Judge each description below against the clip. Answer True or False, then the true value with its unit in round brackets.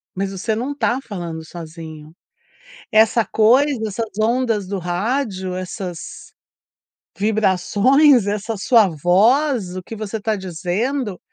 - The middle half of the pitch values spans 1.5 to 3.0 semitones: False (4.3 semitones)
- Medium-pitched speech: False (205 Hz)